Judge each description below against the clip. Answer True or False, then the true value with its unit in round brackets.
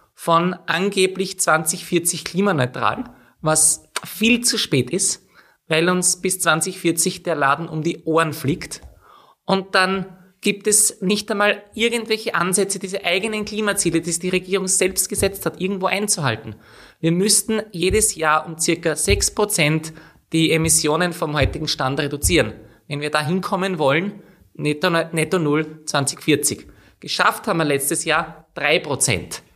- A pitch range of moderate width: True (3.7 semitones)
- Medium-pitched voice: True (170 Hz)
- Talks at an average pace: True (135 wpm)